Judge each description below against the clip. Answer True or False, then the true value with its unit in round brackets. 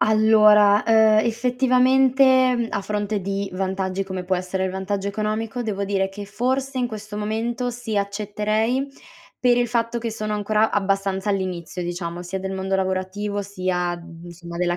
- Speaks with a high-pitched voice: True (205 Hz)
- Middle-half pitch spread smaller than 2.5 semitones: False (2.8 semitones)